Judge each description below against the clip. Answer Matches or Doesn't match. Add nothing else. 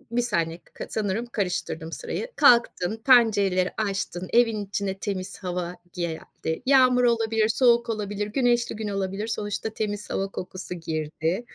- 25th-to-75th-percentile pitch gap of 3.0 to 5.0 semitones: Matches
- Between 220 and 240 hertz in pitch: Doesn't match